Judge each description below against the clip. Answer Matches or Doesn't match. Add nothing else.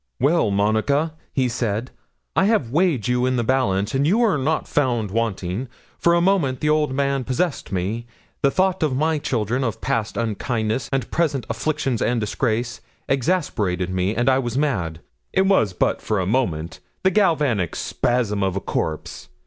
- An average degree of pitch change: Doesn't match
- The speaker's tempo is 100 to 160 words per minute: Doesn't match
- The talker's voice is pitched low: Matches